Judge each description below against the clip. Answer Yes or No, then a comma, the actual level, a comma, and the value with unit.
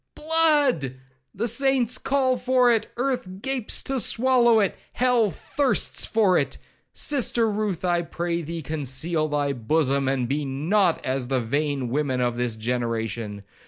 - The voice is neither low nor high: Yes, medium, 170 Hz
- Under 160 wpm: Yes, average, 140 wpm